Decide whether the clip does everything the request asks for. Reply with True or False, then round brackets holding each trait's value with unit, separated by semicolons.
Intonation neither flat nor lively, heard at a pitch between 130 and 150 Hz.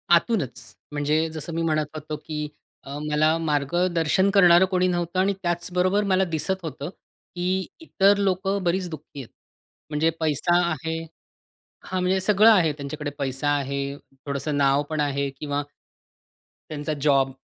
False (4.0 semitones; 160 Hz)